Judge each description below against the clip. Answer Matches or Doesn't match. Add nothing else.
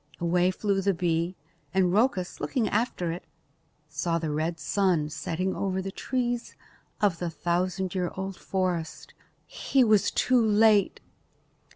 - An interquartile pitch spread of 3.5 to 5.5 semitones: Doesn't match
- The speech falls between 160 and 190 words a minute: Doesn't match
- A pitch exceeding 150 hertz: Matches